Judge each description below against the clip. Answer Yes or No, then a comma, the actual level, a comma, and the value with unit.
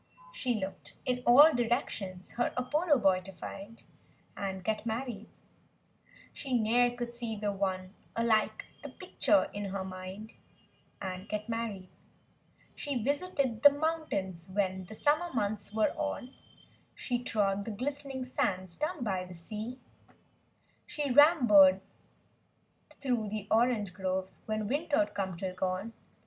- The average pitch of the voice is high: Yes, high, 220 Hz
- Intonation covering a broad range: No, average, 4.8 semitones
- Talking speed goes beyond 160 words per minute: No, slow, 135 wpm